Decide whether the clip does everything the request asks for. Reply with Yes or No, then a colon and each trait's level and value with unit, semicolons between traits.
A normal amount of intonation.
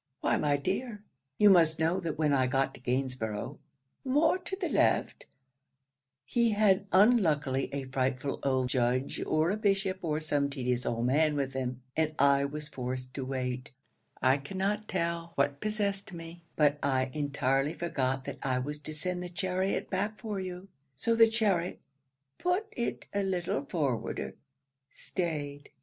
No: wide, 6.1 semitones